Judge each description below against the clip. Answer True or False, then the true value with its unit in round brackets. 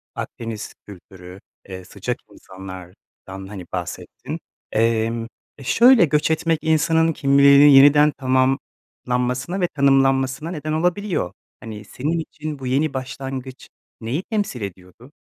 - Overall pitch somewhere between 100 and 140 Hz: True (135 Hz)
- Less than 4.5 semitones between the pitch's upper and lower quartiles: False (5.5 semitones)